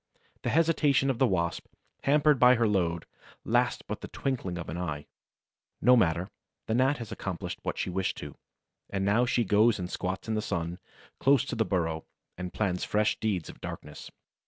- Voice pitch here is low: Yes, low, 105 Hz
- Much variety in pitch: Yes, wide, 5.8 semitones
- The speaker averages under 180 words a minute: No, average, 185 wpm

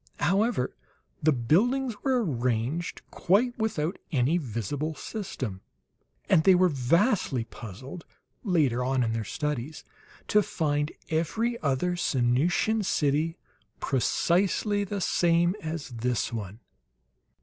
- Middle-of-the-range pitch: Yes, medium, 155 Hz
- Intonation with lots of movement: Yes, wide, 6.9 semitones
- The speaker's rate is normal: No, slow, 110 wpm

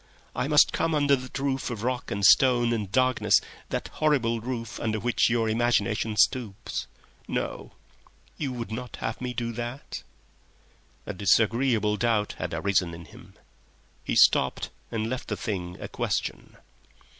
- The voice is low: Yes, low, 115 Hz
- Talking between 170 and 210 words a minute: No, average, 150 wpm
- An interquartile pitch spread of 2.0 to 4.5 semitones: Yes, average, 3.1 semitones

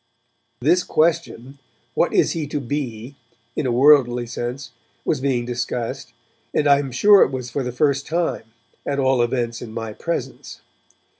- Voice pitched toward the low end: Yes, low, 130 Hz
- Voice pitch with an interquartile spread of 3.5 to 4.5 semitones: No, average, 3.1 semitones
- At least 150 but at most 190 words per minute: Yes, average, 165 wpm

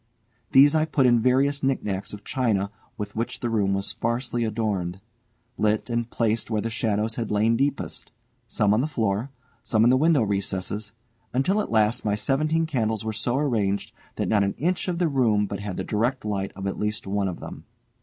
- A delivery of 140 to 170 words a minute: No, fast, 205 wpm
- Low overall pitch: Yes, low, 110 Hz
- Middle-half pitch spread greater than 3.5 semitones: Yes, average, 4.0 semitones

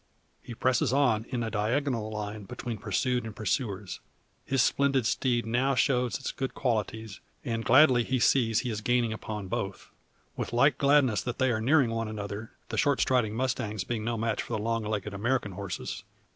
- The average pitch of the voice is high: No, low, 115 Hz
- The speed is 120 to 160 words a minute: No, average, 185 wpm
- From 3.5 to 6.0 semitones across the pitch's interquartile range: No, average, 3.1 semitones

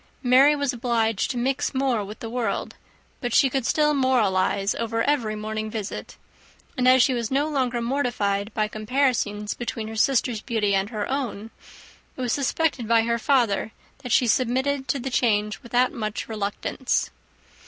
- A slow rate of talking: No, average, 165 wpm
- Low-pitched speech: No, high, 235 Hz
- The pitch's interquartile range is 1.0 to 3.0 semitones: No, average, 3.4 semitones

